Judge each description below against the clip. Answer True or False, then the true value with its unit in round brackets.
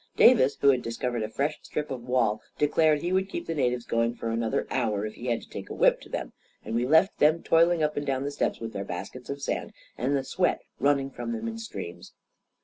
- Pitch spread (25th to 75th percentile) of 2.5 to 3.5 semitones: False (5.1 semitones)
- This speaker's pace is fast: True (240 wpm)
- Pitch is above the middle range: False (135 Hz)